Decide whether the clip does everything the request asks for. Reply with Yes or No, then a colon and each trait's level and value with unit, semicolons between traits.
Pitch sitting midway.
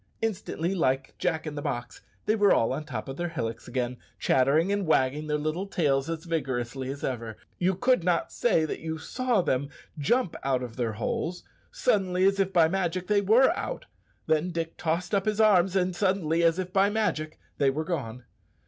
Yes: medium, 165 Hz